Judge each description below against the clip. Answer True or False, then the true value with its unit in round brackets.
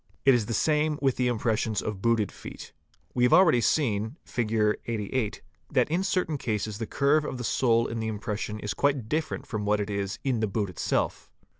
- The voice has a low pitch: True (115 Hz)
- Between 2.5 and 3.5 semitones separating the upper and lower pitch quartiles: False (4.4 semitones)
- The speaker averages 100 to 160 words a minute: False (200 wpm)